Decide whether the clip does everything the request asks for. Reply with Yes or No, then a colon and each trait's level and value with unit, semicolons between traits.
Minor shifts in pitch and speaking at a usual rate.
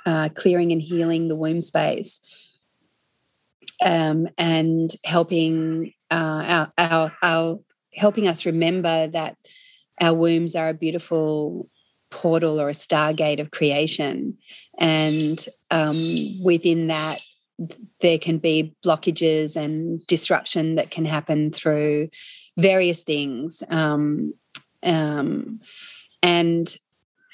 No: narrow, 1.6 semitones; slow, 105 wpm